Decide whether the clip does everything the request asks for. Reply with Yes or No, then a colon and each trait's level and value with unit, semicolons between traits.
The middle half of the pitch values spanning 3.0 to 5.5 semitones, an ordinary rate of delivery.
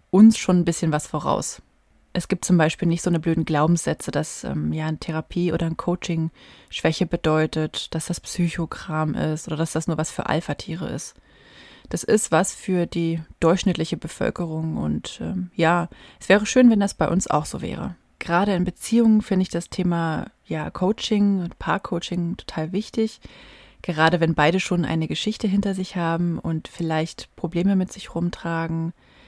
No: narrow, 2.5 semitones; average, 175 wpm